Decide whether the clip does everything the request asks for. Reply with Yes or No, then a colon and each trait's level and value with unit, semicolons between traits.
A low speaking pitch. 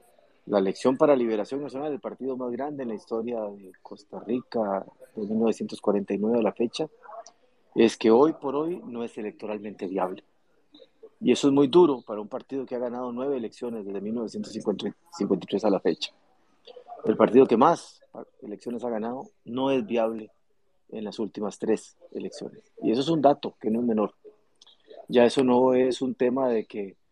Yes: low, 120 Hz